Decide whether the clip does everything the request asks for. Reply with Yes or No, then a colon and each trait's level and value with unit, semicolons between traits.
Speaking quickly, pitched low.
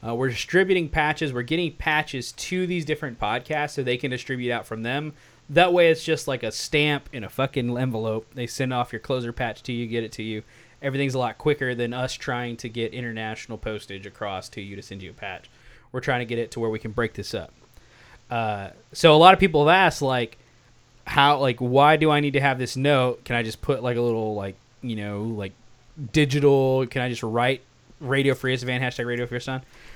Yes: fast, 230 wpm; low, 125 Hz